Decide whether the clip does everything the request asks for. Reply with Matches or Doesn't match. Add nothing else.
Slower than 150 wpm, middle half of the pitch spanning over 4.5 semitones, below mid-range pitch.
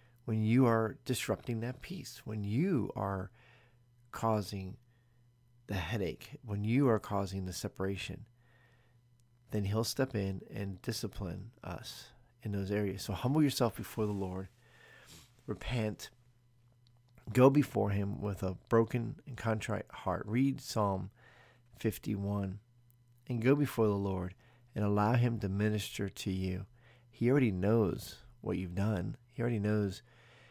Doesn't match